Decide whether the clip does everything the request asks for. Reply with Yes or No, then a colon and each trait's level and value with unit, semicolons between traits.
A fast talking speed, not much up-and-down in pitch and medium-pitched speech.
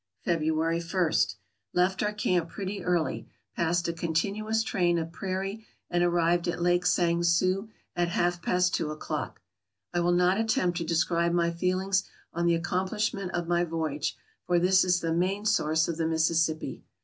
No: average, 170 wpm; narrow, 1.7 semitones; medium, 175 Hz